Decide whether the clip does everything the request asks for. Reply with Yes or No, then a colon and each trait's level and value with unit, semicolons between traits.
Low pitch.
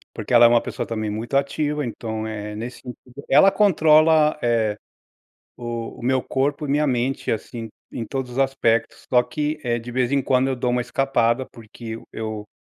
Yes: low, 125 Hz